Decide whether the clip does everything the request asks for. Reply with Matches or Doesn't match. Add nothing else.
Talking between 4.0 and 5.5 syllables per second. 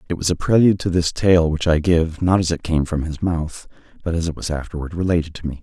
Doesn't match